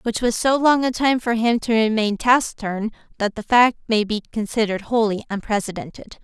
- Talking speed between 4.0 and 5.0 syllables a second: No, 5.6 syllables/s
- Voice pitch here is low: No, high, 225 Hz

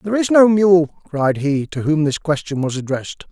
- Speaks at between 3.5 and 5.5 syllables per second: Yes, 5.1 syllables/s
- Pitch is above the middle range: No, medium, 160 Hz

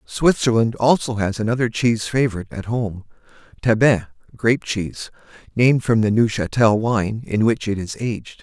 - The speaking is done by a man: Yes, male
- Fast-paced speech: No, average, 140 wpm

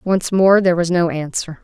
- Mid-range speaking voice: Yes, medium, 175 Hz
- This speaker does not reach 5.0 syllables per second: No, 5.1 syllables/s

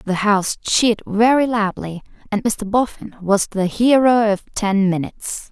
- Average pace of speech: Yes, average, 150 wpm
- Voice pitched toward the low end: No, high, 210 Hz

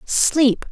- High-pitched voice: Yes, very high, 265 Hz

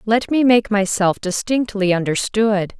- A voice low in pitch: No, high, 210 Hz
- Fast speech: No, slow, 130 wpm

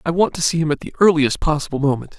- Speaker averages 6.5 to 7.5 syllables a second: Yes, 6.8 syllables/s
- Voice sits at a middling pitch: Yes, medium, 155 Hz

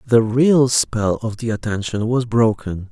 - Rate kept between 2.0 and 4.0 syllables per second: Yes, 3.9 syllables/s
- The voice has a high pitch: No, low, 115 Hz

